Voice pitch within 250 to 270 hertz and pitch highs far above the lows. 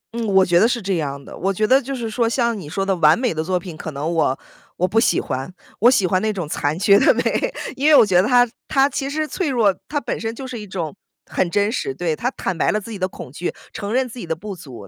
No: high, 200 Hz; wide, 5.7 semitones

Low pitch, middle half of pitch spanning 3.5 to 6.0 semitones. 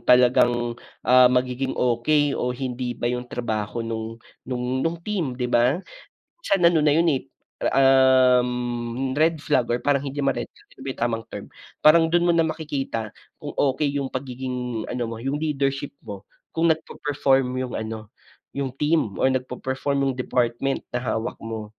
No: low, 130 Hz; average, 2.7 semitones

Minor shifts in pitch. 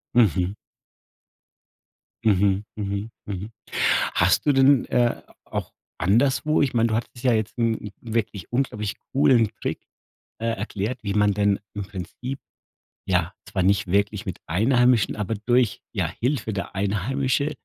No: average, 3.6 semitones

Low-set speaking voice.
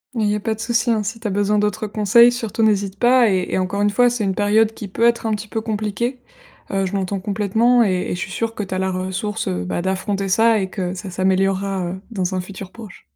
No: high, 205 Hz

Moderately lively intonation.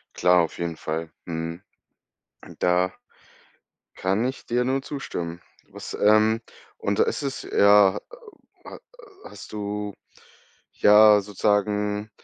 Yes: average, 3.2 semitones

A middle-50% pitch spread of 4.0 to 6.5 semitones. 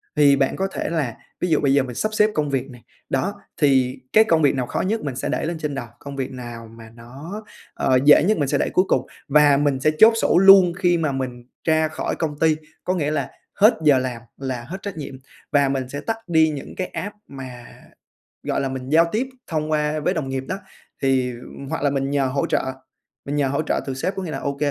No: average, 3.6 semitones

